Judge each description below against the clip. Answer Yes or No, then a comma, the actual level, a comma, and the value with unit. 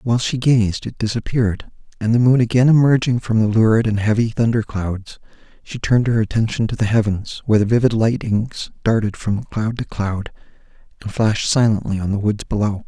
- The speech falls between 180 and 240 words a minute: Yes, average, 185 wpm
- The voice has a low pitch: Yes, low, 110 Hz